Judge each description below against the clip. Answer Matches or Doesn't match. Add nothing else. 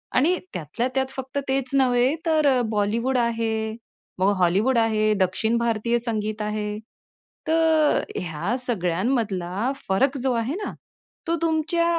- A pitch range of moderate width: Matches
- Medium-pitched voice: Doesn't match